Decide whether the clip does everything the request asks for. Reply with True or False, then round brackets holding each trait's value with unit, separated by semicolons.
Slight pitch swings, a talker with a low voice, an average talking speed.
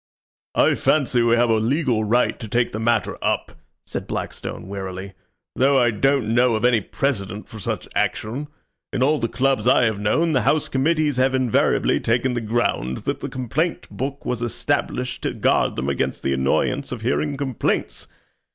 False (3.6 semitones; 120 Hz; 180 wpm)